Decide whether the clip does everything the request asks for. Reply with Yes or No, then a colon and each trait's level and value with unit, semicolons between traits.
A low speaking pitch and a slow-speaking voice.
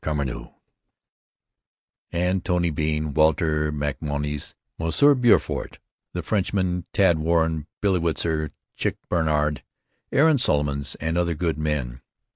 Yes: very low, 80 Hz; slow, 105 wpm